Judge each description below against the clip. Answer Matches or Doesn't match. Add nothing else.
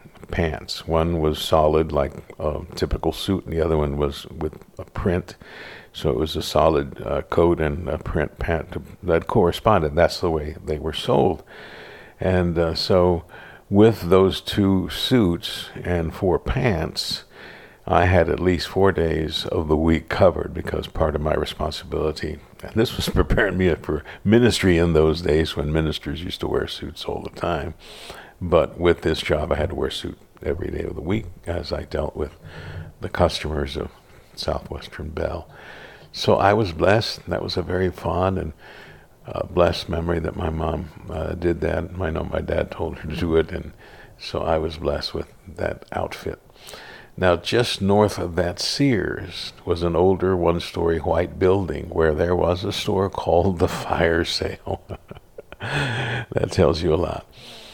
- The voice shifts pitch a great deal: Doesn't match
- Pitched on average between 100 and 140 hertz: Doesn't match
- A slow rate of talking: Doesn't match